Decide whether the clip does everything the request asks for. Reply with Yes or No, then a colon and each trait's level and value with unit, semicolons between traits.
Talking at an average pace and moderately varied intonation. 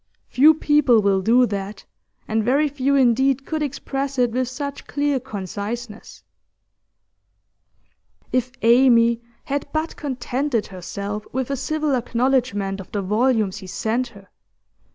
No: slow, 130 wpm; average, 4.4 semitones